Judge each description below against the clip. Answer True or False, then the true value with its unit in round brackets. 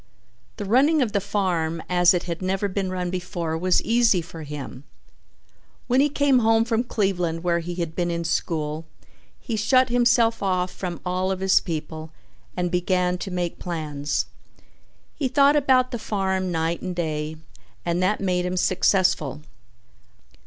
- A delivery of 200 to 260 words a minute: False (160 wpm)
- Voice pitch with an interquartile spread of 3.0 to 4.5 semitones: True (4.0 semitones)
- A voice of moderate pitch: True (180 Hz)